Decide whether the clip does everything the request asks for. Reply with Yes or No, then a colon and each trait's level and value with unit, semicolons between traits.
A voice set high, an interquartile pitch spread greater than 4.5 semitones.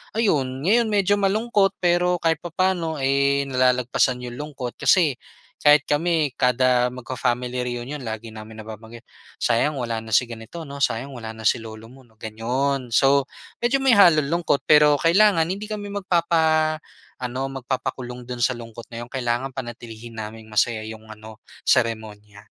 No: low, 130 Hz; wide, 5.5 semitones